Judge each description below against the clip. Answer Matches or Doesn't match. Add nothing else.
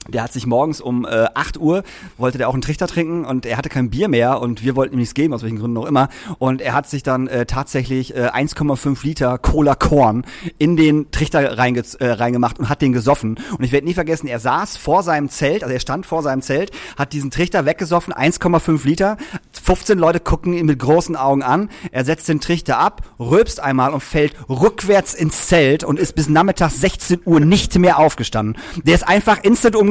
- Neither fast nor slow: Doesn't match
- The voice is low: Doesn't match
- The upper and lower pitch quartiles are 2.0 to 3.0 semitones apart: Doesn't match